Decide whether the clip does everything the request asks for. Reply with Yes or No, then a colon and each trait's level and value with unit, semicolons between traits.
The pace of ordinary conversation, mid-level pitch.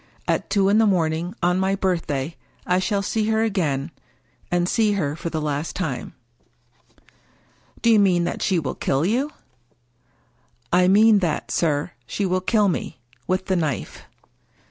Yes: average, 175 wpm; medium, 180 Hz